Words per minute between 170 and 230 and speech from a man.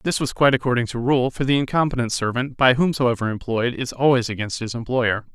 Yes: average, 200 wpm; male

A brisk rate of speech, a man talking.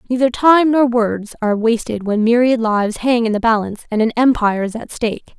No: fast, 210 wpm; female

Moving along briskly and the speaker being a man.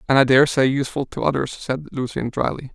No: average, 195 wpm; male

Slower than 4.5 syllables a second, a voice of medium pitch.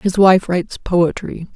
Yes: 4.1 syllables/s; medium, 180 Hz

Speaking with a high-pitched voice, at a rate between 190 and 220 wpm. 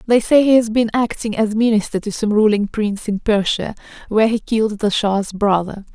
Yes: high, 215 Hz; average, 200 wpm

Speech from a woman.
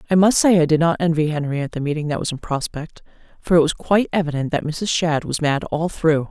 Yes: female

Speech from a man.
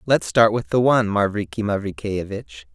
Yes: male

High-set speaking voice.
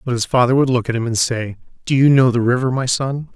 No: low, 125 Hz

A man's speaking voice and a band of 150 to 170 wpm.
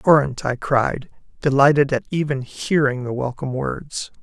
Yes: male; average, 155 wpm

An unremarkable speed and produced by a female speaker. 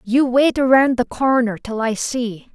Yes: average, 190 wpm; female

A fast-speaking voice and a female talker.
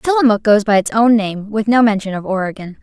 Yes: fast, 235 wpm; female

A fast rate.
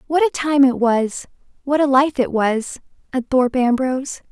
No: average, 165 wpm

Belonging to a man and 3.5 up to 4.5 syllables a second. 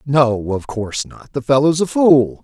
Yes: male; 4.3 syllables/s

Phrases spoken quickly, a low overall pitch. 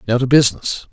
No: average, 195 wpm; low, 125 Hz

